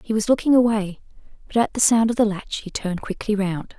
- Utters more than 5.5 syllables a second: Yes, 5.9 syllables/s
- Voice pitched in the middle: No, high, 215 Hz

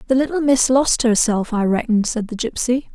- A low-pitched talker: No, high, 240 Hz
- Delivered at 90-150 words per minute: No, fast, 205 wpm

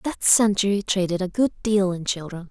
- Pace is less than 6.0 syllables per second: Yes, 4.9 syllables/s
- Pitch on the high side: Yes, high, 195 Hz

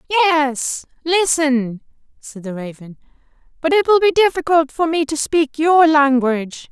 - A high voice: Yes, very high, 300 Hz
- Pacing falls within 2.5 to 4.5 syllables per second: Yes, 4.1 syllables/s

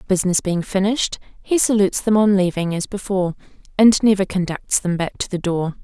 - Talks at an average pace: Yes, average, 195 wpm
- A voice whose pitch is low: No, high, 195 Hz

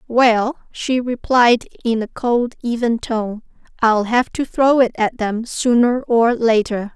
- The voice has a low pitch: No, high, 235 Hz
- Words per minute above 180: No, average, 155 wpm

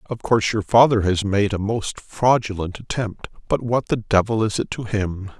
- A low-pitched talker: Yes, low, 105 Hz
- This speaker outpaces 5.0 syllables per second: No, 4.9 syllables/s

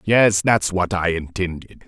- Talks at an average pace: Yes, average, 160 wpm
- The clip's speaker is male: Yes, male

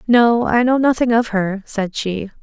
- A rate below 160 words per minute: No, average, 200 wpm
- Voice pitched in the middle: No, high, 225 Hz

